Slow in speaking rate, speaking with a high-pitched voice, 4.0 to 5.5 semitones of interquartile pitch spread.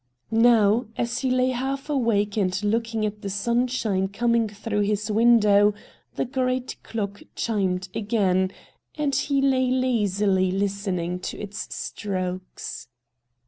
No: slow, 125 wpm; high, 215 Hz; average, 3.4 semitones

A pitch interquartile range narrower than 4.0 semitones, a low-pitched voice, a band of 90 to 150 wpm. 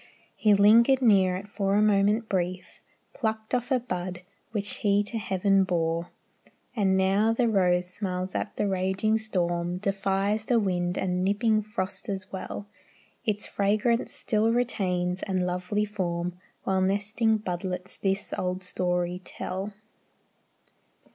No: average, 2.7 semitones; high, 195 Hz; slow, 135 wpm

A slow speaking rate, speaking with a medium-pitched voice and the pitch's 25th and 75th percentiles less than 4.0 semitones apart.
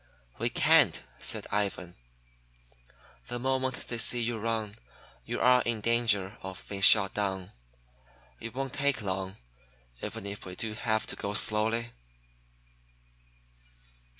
No: slow, 125 wpm; low, 110 Hz; average, 2.9 semitones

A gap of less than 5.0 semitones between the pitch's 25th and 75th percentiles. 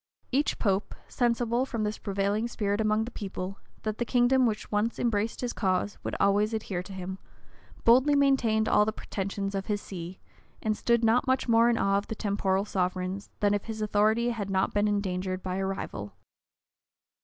Yes: average, 2.9 semitones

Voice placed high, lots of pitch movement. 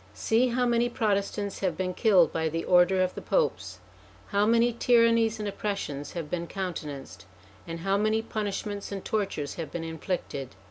No: high, 195 Hz; average, 4.7 semitones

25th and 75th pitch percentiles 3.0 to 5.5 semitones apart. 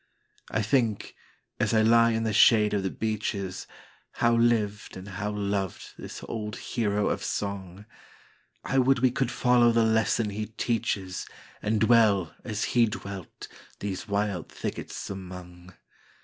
No: narrow, 2.6 semitones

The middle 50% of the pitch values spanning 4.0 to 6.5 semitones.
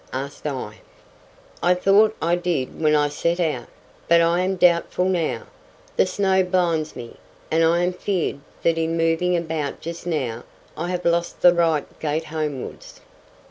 No: narrow, 2.5 semitones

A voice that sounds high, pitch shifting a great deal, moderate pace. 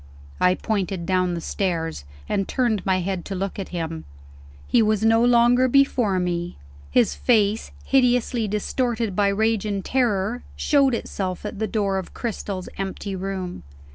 No: high, 200 Hz; average, 3.9 semitones; average, 155 wpm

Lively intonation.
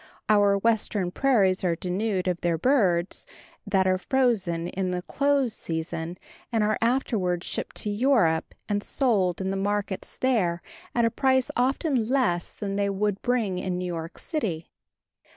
No: average, 4.7 semitones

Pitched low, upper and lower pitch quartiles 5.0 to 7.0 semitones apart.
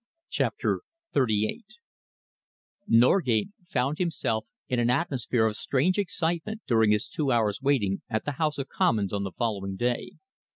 Yes: low, 125 Hz; average, 5.3 semitones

